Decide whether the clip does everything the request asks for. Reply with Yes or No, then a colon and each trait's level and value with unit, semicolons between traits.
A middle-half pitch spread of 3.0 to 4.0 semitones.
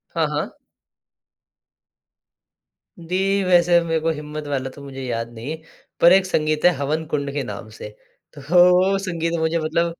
Yes: average, 3.7 semitones